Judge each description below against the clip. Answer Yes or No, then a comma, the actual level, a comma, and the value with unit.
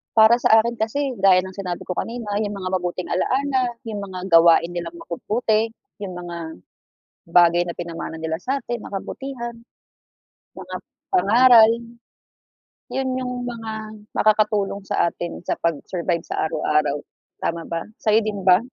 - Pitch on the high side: Yes, high, 200 Hz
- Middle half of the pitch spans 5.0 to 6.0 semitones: Yes, average, 5.3 semitones